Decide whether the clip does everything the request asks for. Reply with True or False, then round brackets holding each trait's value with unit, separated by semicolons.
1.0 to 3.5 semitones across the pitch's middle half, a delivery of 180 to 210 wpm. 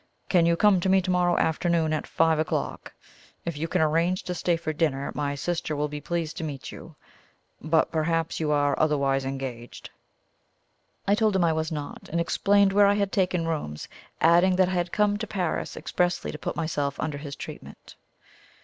True (3.1 semitones; 190 wpm)